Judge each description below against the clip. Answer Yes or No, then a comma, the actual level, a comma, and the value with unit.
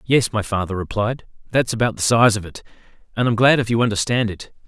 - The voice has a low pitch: Yes, low, 110 Hz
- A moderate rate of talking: No, fast, 220 wpm